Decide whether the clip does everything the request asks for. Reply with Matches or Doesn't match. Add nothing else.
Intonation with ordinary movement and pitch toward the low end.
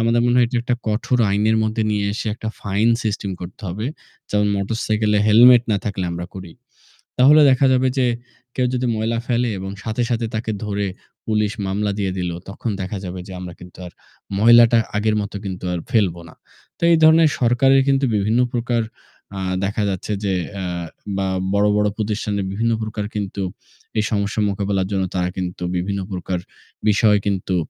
Matches